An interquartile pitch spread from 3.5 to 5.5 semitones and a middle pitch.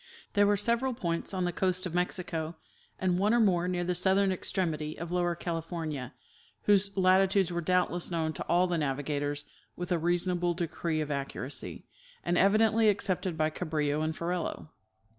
No: average, 2.8 semitones; medium, 175 Hz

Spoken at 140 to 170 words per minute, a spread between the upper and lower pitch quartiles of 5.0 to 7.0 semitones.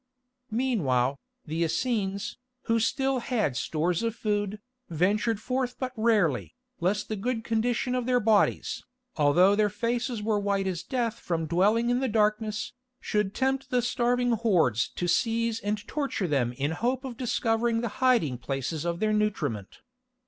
Yes: average, 155 wpm; average, 5.3 semitones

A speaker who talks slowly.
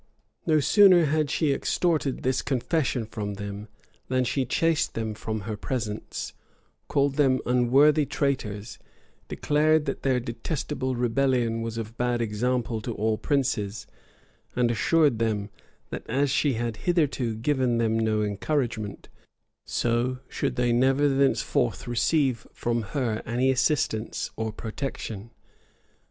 Yes: slow, 130 wpm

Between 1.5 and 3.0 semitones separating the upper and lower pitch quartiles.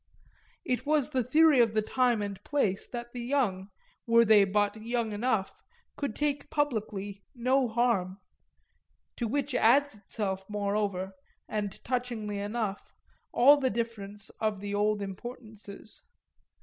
No: average, 3.7 semitones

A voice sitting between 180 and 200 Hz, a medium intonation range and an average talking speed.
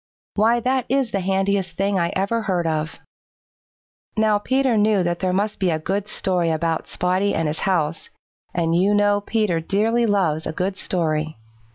Yes: high, 190 Hz; average, 3.6 semitones; average, 175 wpm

